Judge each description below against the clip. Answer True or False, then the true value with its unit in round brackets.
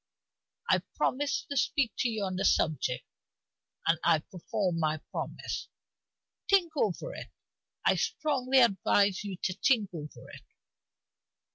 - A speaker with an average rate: False (130 wpm)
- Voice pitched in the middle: False (205 Hz)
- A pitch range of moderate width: False (7.2 semitones)